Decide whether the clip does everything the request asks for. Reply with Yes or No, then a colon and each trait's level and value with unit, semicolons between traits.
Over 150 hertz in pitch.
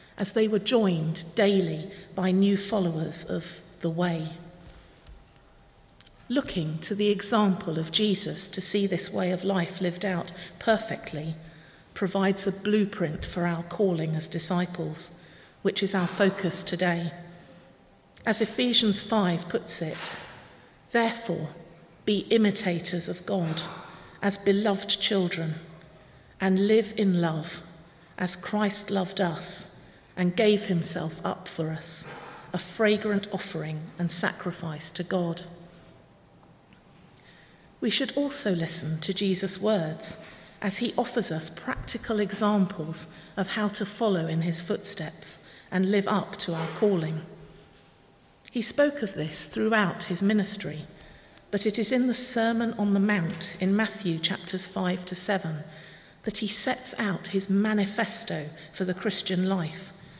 Yes: high, 190 Hz